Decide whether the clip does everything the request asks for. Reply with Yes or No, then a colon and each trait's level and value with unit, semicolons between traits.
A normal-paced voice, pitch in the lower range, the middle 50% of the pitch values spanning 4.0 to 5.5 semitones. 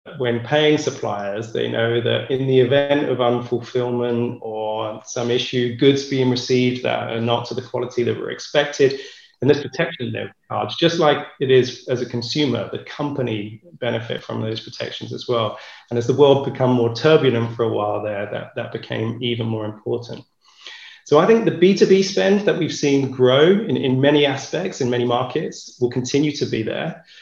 No: average, 185 wpm; low, 125 Hz; average, 3.5 semitones